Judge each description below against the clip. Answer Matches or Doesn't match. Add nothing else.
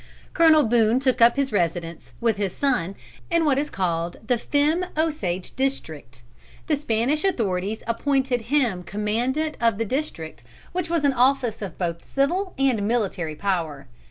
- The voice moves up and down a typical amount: Doesn't match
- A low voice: Doesn't match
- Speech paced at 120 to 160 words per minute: Matches